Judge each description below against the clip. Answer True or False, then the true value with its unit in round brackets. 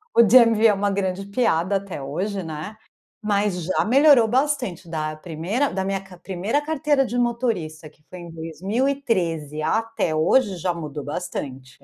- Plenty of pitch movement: True (6.1 semitones)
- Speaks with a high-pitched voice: True (195 Hz)